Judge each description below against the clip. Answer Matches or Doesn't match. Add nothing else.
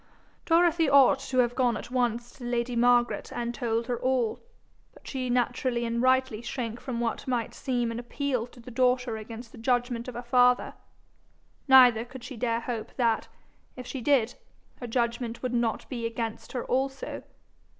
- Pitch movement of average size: Doesn't match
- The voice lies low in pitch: Doesn't match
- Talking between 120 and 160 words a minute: Doesn't match